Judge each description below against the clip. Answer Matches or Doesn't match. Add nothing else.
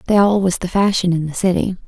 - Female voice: Matches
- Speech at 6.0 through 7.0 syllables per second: Matches